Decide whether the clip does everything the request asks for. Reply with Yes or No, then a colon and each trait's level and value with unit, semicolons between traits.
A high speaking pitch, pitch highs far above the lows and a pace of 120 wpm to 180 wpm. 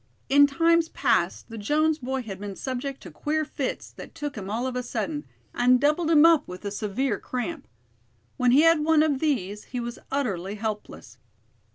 No: very high, 265 Hz; wide, 5.8 semitones; average, 190 wpm